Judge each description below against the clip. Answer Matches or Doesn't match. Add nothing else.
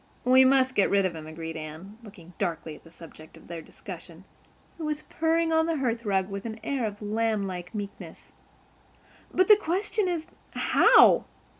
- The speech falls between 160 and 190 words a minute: Matches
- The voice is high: Matches